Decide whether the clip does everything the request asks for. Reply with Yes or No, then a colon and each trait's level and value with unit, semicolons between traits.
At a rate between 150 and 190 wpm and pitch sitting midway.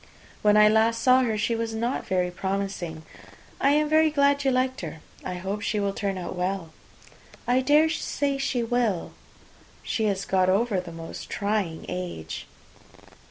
No: average, 165 wpm; high, 210 Hz